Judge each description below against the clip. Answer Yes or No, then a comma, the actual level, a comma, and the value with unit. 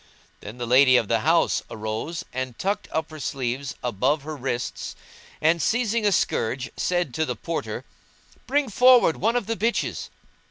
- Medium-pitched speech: Yes, medium, 150 Hz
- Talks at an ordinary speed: Yes, average, 165 wpm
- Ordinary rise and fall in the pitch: No, wide, 8.6 semitones